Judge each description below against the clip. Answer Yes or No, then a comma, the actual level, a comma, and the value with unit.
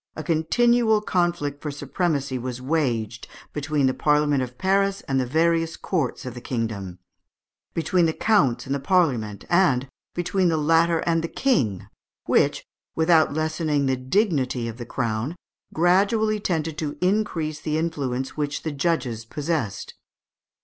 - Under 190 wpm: Yes, average, 145 wpm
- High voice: No, medium, 155 Hz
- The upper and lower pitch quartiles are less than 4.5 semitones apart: No, average, 4.9 semitones